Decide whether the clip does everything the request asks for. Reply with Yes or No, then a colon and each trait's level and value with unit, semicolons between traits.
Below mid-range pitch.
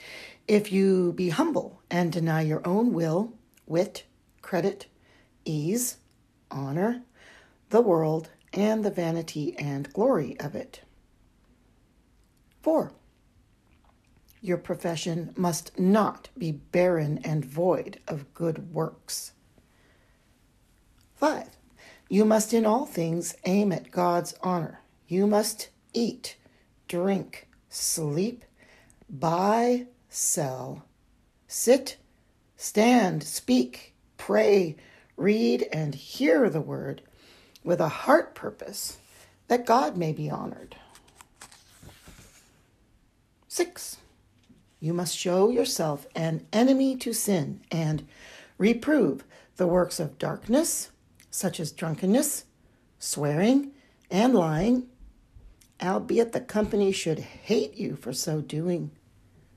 No: medium, 180 Hz